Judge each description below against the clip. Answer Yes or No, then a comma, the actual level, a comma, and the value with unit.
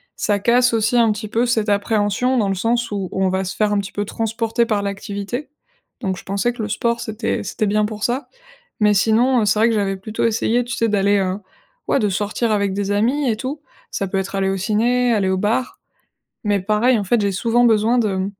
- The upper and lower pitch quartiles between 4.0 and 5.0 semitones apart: No, average, 2.7 semitones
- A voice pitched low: No, high, 215 Hz